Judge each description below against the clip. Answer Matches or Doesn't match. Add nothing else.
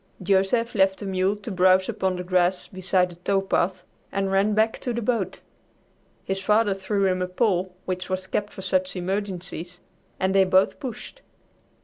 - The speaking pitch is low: Doesn't match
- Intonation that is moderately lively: Doesn't match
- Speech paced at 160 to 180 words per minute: Matches